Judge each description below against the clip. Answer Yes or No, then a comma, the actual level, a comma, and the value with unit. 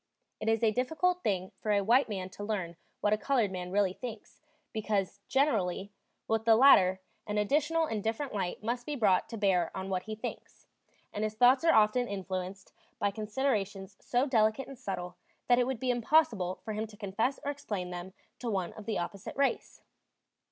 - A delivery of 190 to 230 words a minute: Yes, average, 195 wpm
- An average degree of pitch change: Yes, average, 4.3 semitones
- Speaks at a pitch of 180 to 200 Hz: No, high, 215 Hz